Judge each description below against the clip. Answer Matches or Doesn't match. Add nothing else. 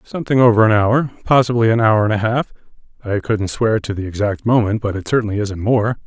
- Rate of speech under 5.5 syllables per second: Doesn't match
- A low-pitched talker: Matches